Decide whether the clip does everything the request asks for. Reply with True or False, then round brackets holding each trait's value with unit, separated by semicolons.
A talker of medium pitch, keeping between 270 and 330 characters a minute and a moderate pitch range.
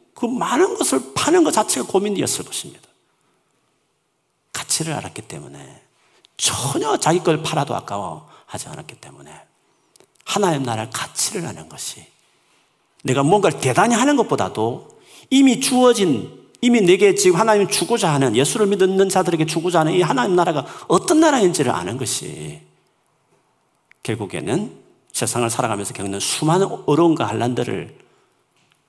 False (175 Hz; 315 characters per minute; 8.7 semitones)